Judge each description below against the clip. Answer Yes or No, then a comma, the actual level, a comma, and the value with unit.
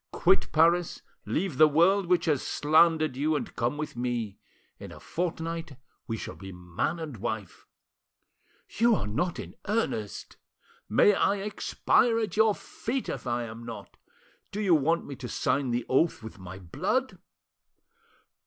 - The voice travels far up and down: Yes, wide, 6.9 semitones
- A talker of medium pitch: Yes, medium, 155 Hz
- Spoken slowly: No, average, 155 wpm